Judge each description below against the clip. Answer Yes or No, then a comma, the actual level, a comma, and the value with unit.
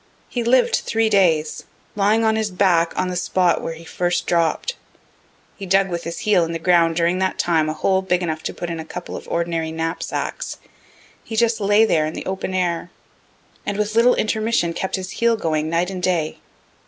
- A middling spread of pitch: Yes, average, 3.7 semitones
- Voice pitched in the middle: Yes, medium, 180 Hz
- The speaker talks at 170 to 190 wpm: No, fast, 205 wpm